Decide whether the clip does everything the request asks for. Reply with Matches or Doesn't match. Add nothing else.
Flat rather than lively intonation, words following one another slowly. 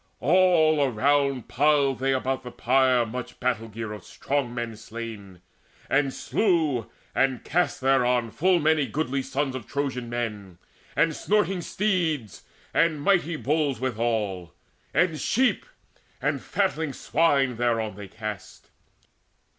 Doesn't match